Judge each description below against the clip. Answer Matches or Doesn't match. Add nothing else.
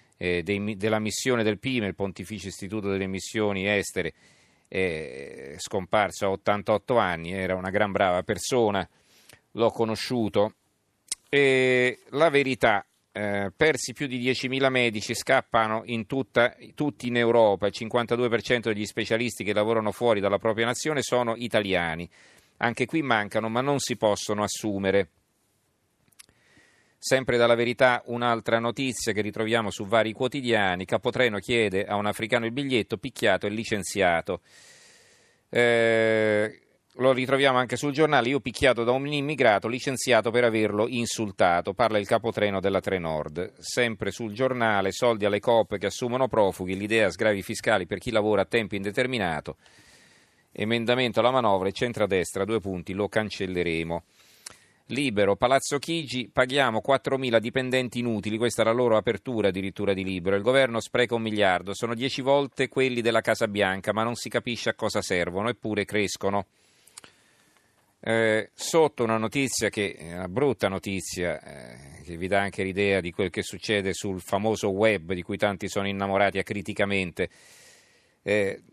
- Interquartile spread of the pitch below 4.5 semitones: Matches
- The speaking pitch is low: Matches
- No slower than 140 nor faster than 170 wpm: Matches